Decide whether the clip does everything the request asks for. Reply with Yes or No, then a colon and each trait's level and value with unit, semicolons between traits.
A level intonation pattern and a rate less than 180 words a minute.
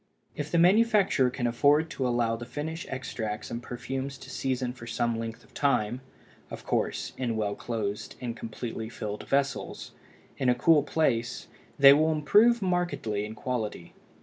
No: average, 4.3 semitones; average, 150 wpm